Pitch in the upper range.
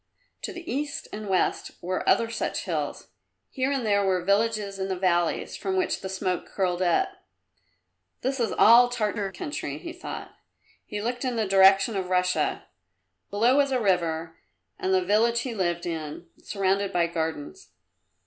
Yes: high, 195 Hz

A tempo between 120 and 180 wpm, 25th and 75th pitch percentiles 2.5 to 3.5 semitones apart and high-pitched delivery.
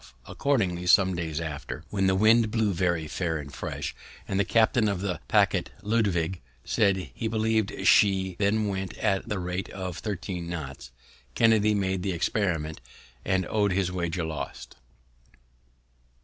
No: average, 150 wpm; average, 3.2 semitones; very low, 95 Hz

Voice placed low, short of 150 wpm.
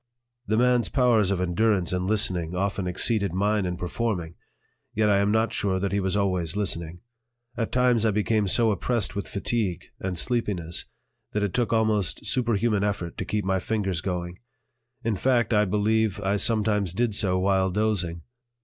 No: low, 100 Hz; average, 170 wpm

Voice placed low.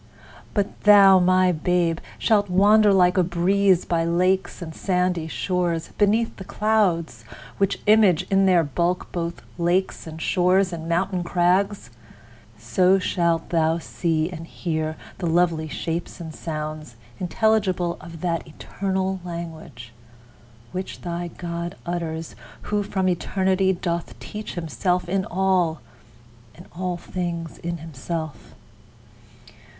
No: medium, 175 Hz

